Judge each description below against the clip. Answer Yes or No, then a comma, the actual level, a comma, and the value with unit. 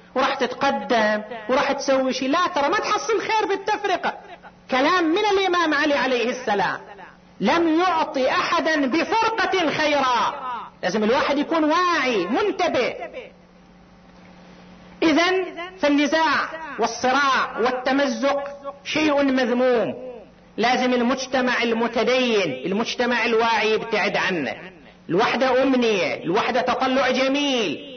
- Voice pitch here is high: Yes, very high, 275 Hz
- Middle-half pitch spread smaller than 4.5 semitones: No, average, 5.2 semitones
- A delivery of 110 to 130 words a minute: No, average, 95 wpm